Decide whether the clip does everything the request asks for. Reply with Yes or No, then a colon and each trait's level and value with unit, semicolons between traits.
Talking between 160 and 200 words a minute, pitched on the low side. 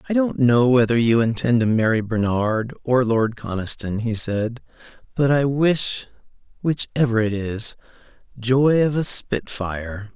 No: average, 150 wpm; low, 120 Hz